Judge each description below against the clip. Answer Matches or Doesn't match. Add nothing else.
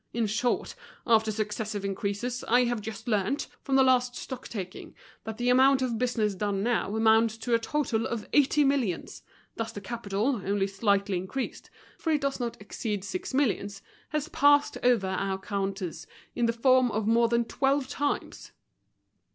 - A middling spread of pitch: Matches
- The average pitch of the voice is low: Doesn't match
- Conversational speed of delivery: Matches